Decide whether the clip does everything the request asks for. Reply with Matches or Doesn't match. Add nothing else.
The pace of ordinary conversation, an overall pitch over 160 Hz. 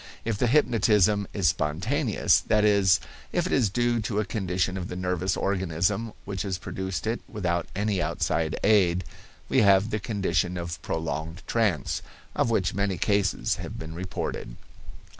Doesn't match